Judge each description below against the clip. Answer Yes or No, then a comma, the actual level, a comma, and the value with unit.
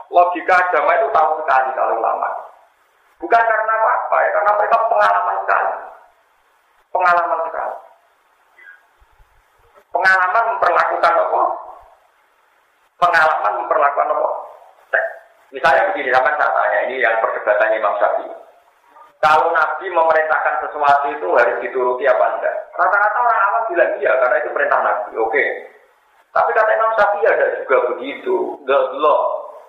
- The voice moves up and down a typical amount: No, wide, 6.6 semitones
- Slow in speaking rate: No, average, 125 wpm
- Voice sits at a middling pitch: No, high, 195 Hz